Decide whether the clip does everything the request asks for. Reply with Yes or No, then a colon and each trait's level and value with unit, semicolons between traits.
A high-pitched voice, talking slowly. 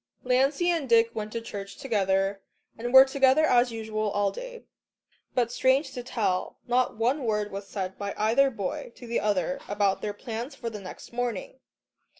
No: high, 230 Hz; average, 175 wpm